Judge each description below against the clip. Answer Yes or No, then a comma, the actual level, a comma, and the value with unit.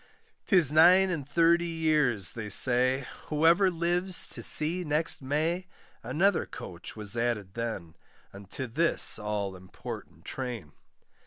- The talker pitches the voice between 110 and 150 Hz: Yes, medium, 140 Hz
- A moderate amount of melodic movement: No, wide, 7.4 semitones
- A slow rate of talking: Yes, slow, 120 wpm